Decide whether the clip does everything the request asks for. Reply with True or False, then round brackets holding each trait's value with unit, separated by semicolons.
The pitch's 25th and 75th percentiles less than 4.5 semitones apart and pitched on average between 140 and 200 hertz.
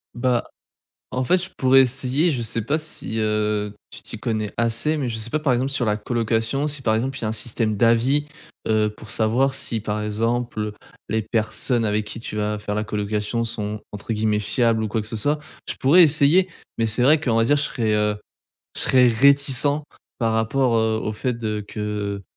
False (3.4 semitones; 115 Hz)